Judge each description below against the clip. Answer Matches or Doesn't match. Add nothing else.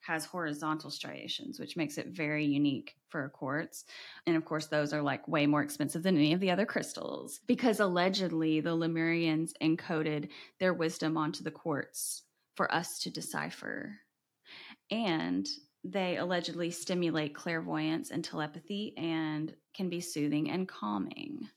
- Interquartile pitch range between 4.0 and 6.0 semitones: Doesn't match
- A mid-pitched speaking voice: Matches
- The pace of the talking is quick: Doesn't match